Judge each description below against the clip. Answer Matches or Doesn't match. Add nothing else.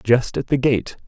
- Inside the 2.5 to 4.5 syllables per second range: Matches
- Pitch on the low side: Matches